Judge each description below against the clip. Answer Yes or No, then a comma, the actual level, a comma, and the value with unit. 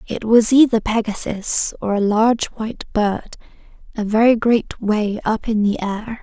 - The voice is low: No, high, 220 Hz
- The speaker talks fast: No, average, 165 wpm